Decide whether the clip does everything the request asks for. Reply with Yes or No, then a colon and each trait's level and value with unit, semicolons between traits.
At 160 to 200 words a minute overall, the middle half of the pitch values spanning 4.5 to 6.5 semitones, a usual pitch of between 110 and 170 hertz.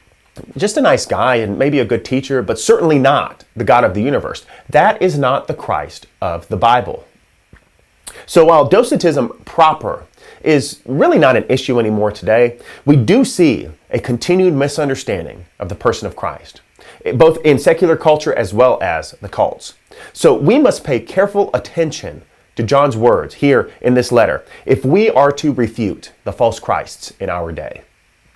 Yes: average, 170 wpm; wide, 5.4 semitones; medium, 140 Hz